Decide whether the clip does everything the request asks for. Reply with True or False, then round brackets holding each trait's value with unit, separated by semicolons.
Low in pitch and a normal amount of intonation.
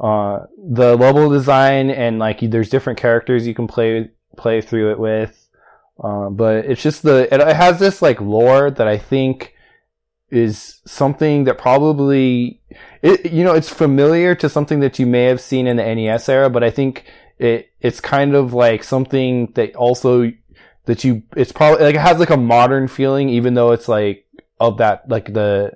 True (125 Hz; 3.4 semitones)